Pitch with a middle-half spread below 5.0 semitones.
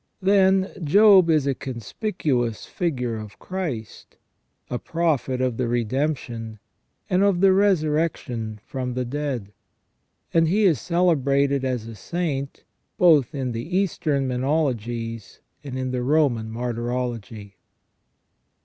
No: wide, 5.5 semitones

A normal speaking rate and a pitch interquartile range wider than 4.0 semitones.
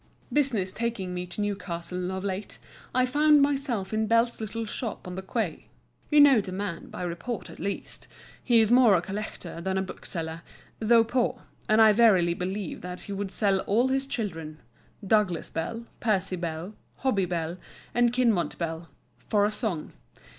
Yes: average, 165 wpm; average, 4.4 semitones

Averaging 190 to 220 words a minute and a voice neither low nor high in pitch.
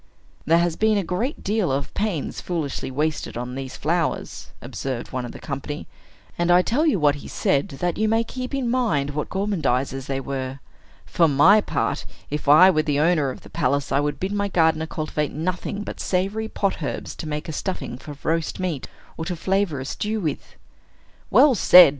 Yes: average, 195 wpm; medium, 160 Hz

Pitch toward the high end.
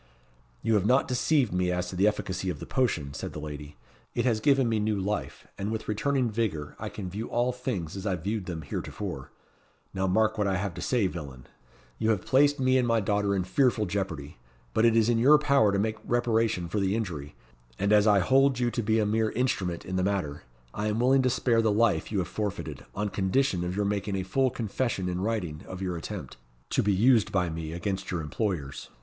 No: low, 105 Hz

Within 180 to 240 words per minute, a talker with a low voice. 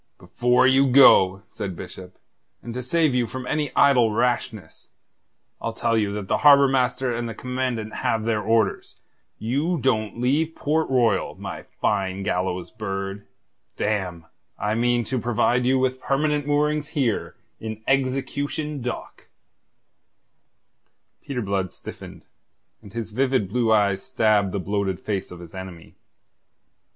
No: average, 140 wpm; low, 115 Hz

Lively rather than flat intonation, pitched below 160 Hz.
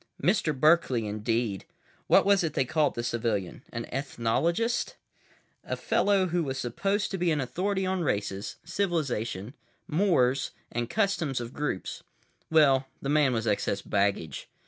Yes: wide, 6.9 semitones; low, 135 Hz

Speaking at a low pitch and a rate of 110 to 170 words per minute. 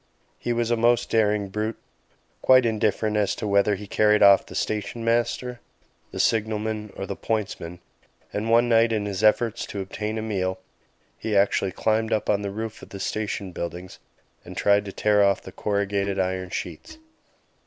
No: low, 105 Hz; average, 180 wpm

